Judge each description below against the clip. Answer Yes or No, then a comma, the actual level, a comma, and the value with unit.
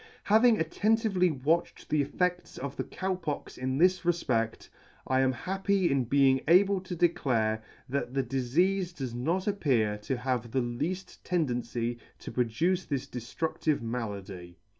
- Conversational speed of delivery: Yes, average, 145 wpm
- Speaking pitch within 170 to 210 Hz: No, medium, 140 Hz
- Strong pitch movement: Yes, wide, 6.7 semitones